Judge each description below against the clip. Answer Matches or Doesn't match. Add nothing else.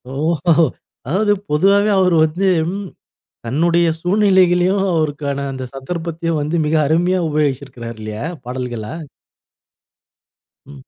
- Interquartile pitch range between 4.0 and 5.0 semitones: Matches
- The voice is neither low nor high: Matches